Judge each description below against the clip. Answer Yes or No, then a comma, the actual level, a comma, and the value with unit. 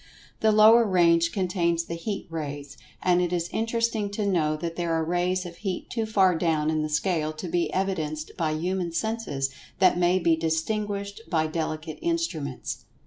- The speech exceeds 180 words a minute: No, average, 175 wpm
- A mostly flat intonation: No, average, 3.9 semitones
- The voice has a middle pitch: Yes, medium, 175 Hz